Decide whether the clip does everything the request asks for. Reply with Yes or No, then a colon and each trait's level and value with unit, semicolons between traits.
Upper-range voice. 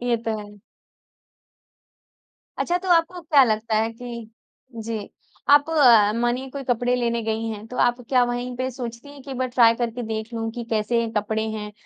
Yes: high, 235 Hz